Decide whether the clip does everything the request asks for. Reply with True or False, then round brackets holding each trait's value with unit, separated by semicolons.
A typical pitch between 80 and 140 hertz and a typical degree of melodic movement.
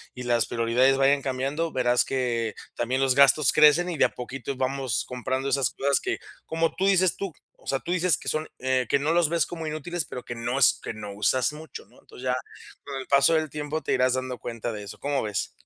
True (135 Hz; 3.7 semitones)